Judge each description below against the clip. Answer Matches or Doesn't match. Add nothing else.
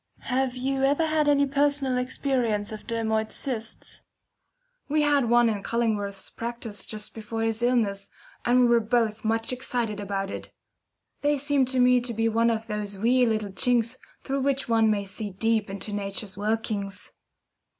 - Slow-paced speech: Doesn't match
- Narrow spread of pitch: Doesn't match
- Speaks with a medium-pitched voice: Doesn't match